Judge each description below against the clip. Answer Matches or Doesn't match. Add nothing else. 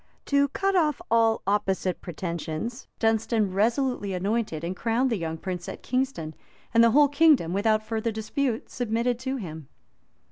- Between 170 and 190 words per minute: Doesn't match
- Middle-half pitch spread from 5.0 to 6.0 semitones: Matches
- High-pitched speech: Matches